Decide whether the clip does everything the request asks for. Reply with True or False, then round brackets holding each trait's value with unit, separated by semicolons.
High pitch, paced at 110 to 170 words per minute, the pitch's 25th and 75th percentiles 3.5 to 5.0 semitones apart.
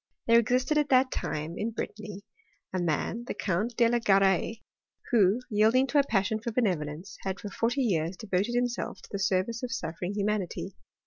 False (215 Hz; 185 wpm; 4.0 semitones)